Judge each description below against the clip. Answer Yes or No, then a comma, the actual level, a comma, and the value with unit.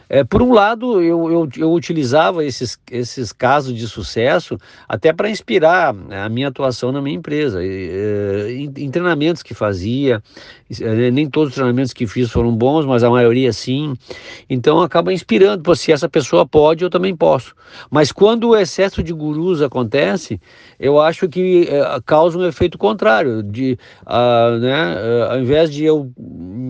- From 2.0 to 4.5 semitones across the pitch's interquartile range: No, wide, 5.5 semitones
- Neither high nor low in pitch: Yes, medium, 145 Hz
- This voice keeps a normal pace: Yes, average, 175 wpm